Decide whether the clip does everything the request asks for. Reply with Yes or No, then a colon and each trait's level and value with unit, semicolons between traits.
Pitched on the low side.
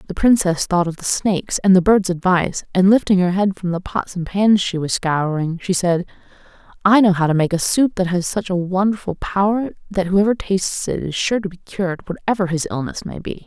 No: medium, 185 Hz